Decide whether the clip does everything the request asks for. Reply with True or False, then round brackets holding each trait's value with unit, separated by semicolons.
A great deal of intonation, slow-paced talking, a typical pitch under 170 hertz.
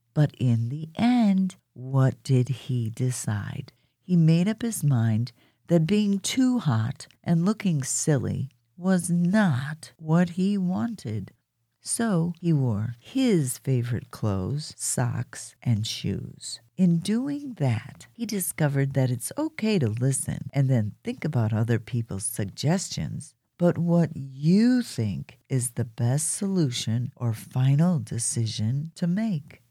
True (6.5 semitones; 130 wpm; 140 Hz)